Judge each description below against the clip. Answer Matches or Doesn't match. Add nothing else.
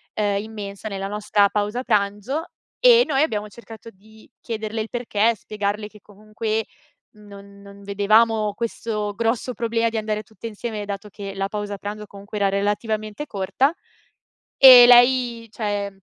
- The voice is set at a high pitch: Matches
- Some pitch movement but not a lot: Doesn't match